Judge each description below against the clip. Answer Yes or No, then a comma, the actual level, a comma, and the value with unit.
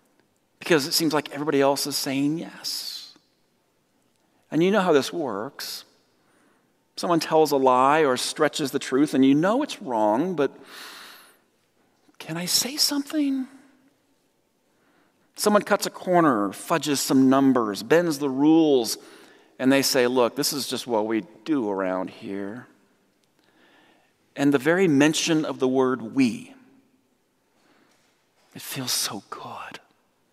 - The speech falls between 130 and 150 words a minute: Yes, slow, 135 wpm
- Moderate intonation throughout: No, wide, 7.5 semitones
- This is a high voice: No, medium, 150 Hz